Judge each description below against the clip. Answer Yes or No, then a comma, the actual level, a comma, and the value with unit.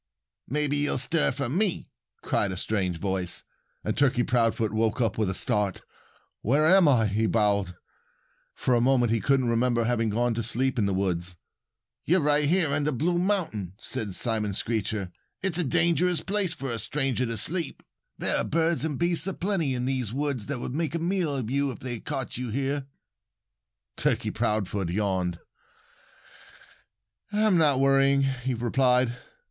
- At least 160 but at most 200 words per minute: Yes, average, 170 wpm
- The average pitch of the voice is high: No, low, 125 Hz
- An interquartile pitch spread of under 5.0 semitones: No, average, 5.3 semitones